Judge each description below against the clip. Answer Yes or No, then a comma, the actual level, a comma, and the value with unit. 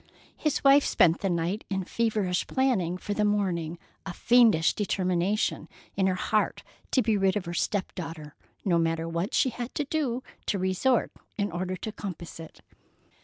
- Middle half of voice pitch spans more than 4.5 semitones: No, average, 4.1 semitones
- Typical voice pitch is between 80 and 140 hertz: No, high, 190 Hz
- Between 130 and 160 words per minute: No, average, 170 wpm